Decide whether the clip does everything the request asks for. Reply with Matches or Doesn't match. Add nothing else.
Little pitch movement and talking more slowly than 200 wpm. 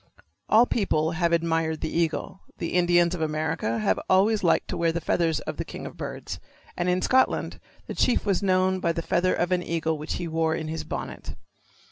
Doesn't match